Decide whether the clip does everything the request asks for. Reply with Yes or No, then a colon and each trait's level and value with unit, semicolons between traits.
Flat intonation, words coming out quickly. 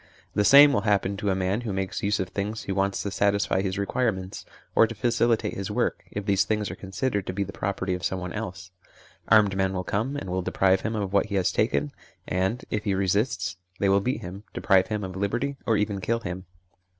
Yes: narrow, 2.1 semitones; fast, 230 wpm